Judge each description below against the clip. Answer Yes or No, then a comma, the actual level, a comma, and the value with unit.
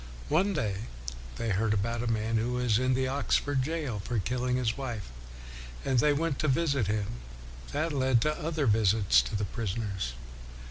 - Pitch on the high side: No, low, 120 Hz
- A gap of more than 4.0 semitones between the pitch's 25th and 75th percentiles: Yes, average, 4.6 semitones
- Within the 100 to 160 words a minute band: No, average, 175 wpm